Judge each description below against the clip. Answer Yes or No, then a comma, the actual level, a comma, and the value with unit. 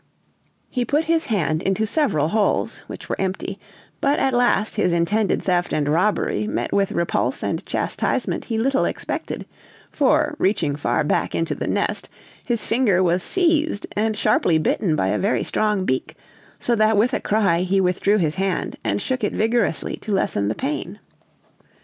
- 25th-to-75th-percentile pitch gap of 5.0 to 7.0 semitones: Yes, wide, 5.4 semitones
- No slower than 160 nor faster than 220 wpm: Yes, average, 170 wpm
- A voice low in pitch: No, high, 210 Hz